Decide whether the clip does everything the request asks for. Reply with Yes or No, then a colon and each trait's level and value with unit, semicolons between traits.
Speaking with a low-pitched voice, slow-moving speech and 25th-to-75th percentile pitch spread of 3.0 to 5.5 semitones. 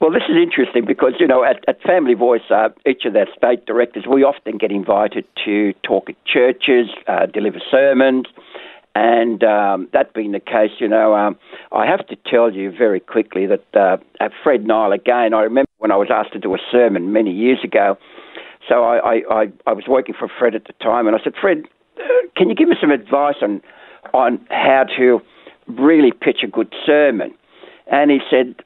No: low, 125 Hz; fast, 205 wpm; average, 5.1 semitones